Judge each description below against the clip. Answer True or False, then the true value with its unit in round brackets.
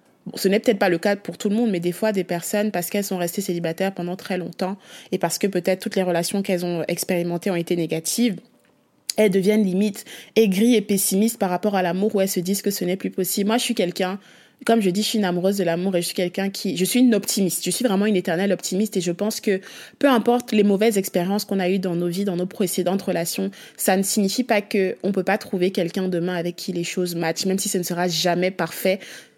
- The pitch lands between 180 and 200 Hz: True (190 Hz)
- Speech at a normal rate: False (255 wpm)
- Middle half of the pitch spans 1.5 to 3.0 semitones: True (2.6 semitones)